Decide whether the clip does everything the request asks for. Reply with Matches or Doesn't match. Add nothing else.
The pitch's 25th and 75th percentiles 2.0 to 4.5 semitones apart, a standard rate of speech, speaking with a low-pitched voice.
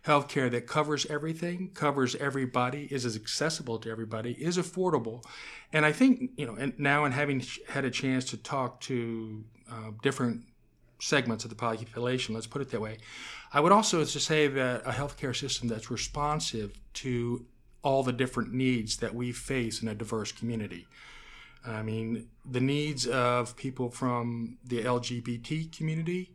Matches